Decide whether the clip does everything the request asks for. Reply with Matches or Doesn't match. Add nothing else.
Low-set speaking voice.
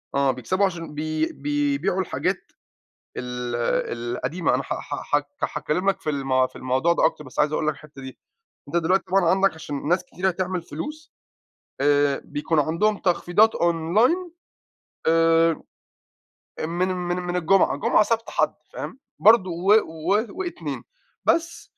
Doesn't match